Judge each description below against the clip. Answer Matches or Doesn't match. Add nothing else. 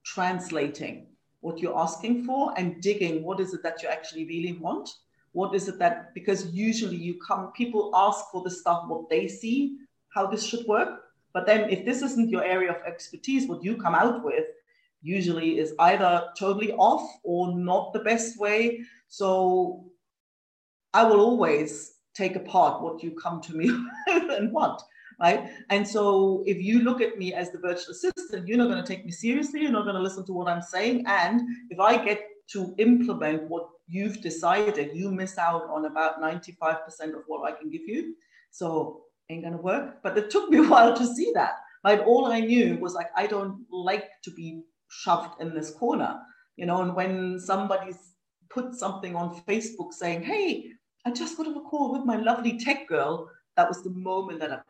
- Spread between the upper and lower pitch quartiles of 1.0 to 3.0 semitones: Doesn't match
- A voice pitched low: Doesn't match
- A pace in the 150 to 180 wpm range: Doesn't match